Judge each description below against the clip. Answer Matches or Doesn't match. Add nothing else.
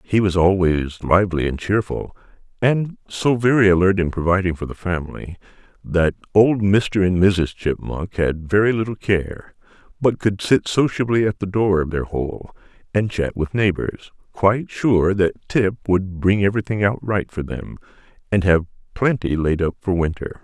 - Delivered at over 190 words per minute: Doesn't match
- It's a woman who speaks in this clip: Doesn't match